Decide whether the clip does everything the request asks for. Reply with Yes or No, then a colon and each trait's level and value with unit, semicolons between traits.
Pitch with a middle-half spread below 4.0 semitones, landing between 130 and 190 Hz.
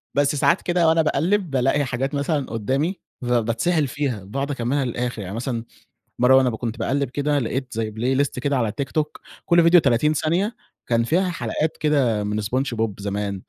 No: average, 4.6 semitones; low, 135 Hz